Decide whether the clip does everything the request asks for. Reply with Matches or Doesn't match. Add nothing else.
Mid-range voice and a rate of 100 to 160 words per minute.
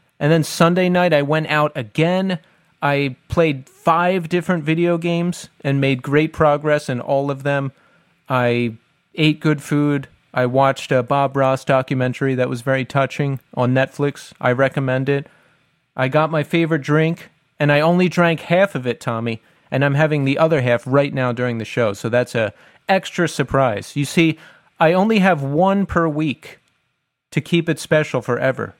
Doesn't match